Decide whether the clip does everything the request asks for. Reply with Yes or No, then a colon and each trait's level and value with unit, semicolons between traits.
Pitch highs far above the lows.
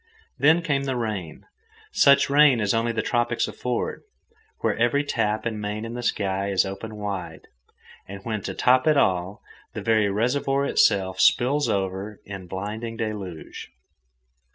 No: average, 4.0 semitones